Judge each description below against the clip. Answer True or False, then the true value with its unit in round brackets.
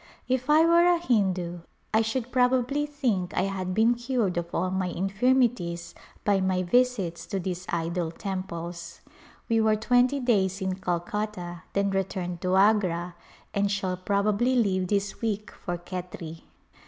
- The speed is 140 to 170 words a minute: True (155 wpm)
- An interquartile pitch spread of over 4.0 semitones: True (4.7 semitones)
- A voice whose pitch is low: False (195 Hz)